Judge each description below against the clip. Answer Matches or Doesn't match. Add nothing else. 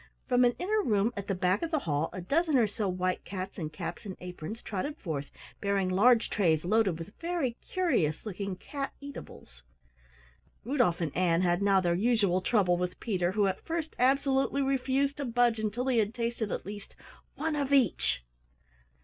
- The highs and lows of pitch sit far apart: Matches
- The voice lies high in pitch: Matches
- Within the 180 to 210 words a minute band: Matches